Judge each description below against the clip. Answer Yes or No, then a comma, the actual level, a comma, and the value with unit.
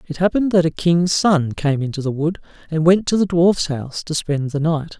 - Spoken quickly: Yes, fast, 240 wpm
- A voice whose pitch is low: No, medium, 165 Hz